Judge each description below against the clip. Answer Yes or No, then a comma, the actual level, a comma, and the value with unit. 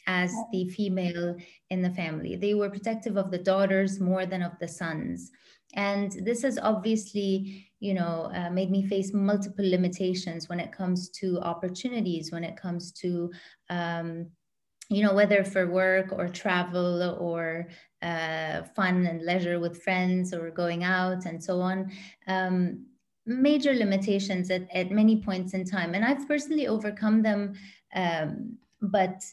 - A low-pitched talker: No, medium, 185 Hz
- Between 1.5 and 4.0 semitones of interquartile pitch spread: Yes, narrow, 2.5 semitones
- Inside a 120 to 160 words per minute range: Yes, average, 155 wpm